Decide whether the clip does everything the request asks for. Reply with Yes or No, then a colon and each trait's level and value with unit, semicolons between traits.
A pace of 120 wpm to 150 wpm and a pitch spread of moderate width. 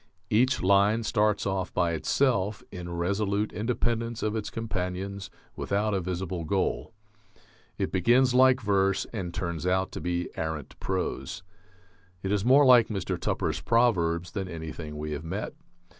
Yes: average, 145 wpm; average, 4.0 semitones